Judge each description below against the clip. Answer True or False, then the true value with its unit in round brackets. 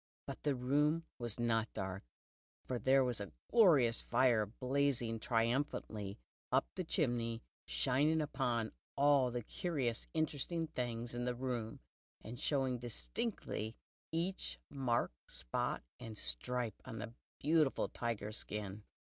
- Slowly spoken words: True (125 wpm)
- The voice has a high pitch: False (120 Hz)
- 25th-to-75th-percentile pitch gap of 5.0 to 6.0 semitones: False (3.8 semitones)